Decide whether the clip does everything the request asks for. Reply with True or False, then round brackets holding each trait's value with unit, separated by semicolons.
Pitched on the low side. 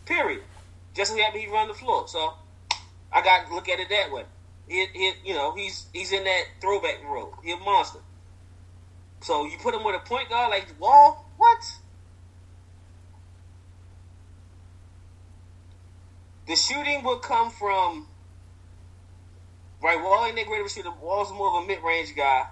True (90 Hz)